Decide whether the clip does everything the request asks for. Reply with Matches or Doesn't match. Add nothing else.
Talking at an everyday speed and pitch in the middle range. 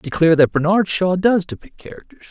Matches